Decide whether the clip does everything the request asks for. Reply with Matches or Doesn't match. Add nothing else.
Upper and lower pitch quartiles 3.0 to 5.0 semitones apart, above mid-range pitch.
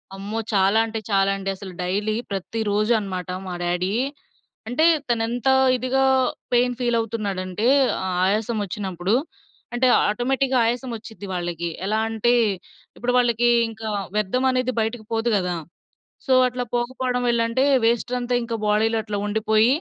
Matches